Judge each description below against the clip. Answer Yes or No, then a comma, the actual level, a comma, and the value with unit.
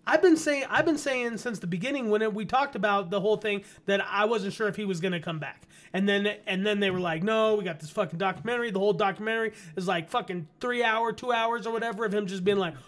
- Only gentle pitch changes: No, average, 3.0 semitones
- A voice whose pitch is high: Yes, high, 210 Hz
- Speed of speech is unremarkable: No, fast, 270 wpm